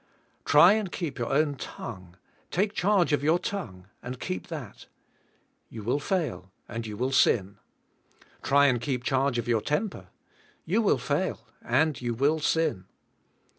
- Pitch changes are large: Yes, wide, 5.9 semitones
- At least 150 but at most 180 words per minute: Yes, average, 160 wpm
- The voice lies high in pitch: No, low, 135 Hz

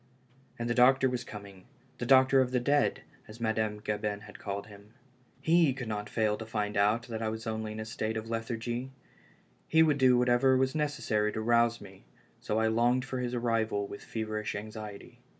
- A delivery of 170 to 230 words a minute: Yes, average, 200 wpm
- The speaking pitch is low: Yes, low, 115 Hz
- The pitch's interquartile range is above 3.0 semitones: No, narrow, 2.6 semitones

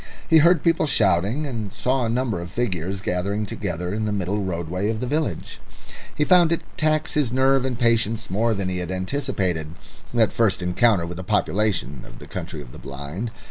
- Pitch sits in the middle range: No, low, 105 Hz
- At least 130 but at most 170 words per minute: No, average, 195 wpm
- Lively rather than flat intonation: Yes, wide, 5.9 semitones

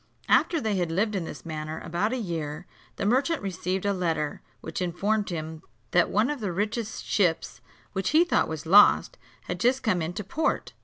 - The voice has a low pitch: No, high, 190 Hz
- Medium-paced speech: Yes, average, 190 wpm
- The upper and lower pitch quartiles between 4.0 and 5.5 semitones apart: Yes, average, 4.7 semitones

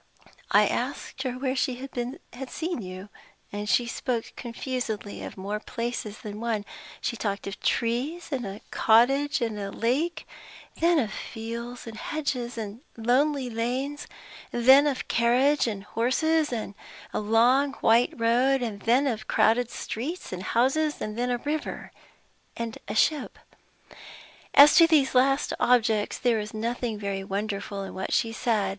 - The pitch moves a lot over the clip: No, average, 3.6 semitones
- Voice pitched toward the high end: Yes, high, 240 Hz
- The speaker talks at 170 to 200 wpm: No, average, 150 wpm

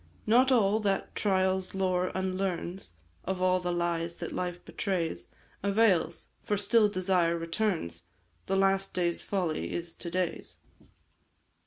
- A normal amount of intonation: No, narrow, 2.2 semitones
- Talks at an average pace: No, slow, 130 wpm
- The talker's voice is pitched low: No, medium, 185 Hz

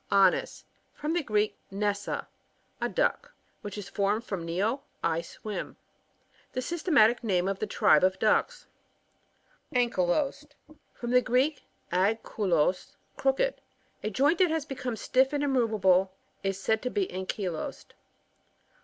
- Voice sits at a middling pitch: No, high, 220 Hz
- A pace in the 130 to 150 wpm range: Yes, average, 140 wpm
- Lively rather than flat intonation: Yes, wide, 6.0 semitones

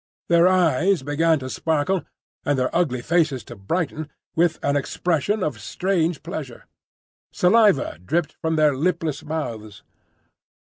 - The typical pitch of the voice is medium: Yes, medium, 160 Hz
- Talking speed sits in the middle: No, slow, 130 wpm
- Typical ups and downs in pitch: Yes, average, 3.8 semitones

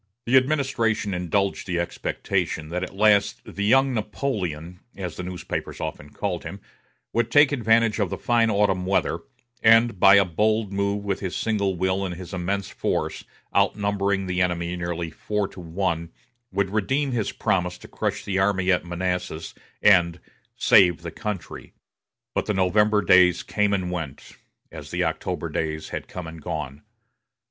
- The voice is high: No, very low, 95 Hz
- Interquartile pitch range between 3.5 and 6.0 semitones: No, average, 3.0 semitones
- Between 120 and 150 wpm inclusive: No, average, 160 wpm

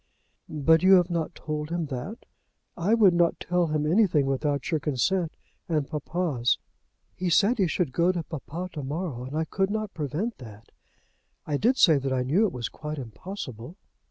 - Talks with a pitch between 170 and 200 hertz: No, medium, 160 Hz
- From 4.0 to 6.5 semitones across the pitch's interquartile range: Yes, average, 4.5 semitones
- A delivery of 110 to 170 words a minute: No, average, 185 wpm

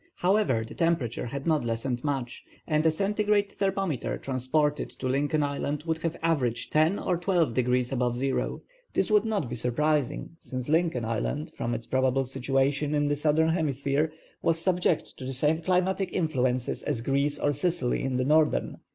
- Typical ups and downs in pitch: Yes, average, 4.3 semitones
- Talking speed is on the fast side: No, average, 170 wpm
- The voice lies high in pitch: No, medium, 145 Hz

